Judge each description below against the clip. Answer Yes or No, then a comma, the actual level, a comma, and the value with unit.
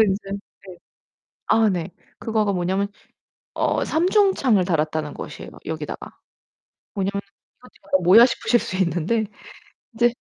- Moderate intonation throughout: Yes, average, 4.1 semitones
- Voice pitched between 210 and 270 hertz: No, high, 200 Hz